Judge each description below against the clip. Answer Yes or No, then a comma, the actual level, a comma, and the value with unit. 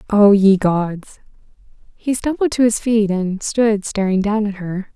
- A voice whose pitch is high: Yes, high, 205 Hz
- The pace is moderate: Yes, average, 170 wpm